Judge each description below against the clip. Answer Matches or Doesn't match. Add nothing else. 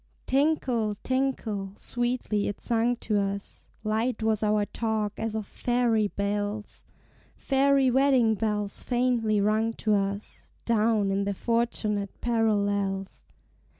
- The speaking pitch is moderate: Doesn't match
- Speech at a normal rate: Doesn't match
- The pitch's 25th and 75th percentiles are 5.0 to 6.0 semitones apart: Doesn't match